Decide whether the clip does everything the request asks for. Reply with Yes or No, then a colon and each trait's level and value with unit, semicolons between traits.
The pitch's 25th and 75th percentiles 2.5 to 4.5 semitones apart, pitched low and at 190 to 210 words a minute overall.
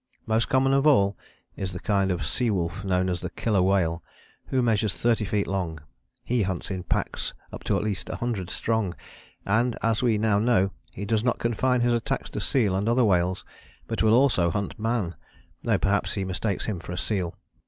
Yes: average, 3.8 semitones; low, 105 Hz; fast, 205 wpm